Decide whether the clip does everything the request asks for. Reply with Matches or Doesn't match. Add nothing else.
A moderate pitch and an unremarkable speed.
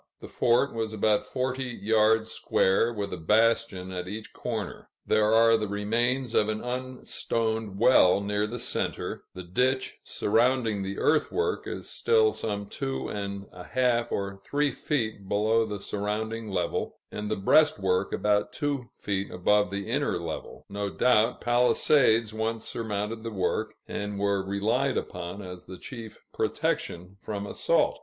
Doesn't match